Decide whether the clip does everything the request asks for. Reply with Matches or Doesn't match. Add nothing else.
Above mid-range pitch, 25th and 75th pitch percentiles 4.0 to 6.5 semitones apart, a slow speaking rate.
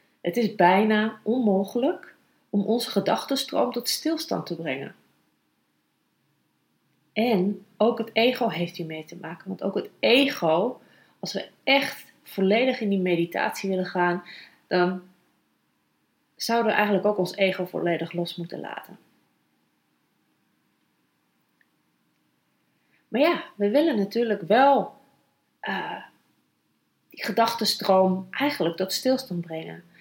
Matches